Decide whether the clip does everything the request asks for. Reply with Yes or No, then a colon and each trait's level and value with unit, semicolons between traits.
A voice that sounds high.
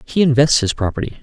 No: low, 130 Hz